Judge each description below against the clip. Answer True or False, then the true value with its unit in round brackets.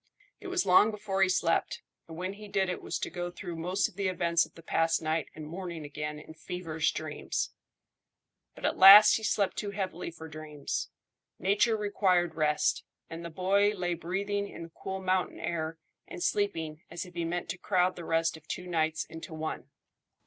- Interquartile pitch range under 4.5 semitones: True (3.0 semitones)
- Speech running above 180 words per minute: True (195 wpm)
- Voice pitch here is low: False (175 Hz)